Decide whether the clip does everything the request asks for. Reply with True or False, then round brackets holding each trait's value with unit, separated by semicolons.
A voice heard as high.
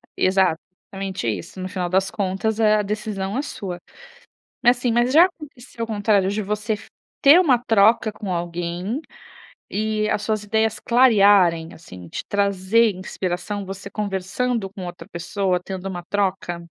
True (200 Hz)